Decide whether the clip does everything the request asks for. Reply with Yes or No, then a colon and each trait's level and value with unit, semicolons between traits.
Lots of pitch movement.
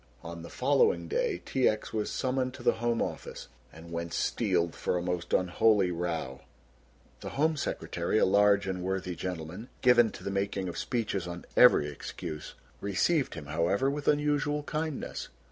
Yes: wide, 6.9 semitones